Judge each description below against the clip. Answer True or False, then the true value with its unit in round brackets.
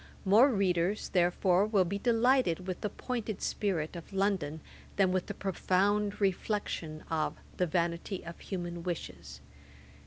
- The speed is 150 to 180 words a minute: False (135 wpm)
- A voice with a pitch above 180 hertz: True (190 Hz)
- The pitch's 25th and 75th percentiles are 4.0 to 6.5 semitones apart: False (3.0 semitones)